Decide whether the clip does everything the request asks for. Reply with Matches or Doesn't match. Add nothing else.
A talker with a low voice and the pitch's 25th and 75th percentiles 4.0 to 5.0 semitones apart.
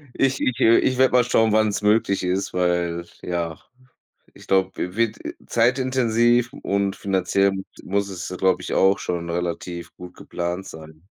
Matches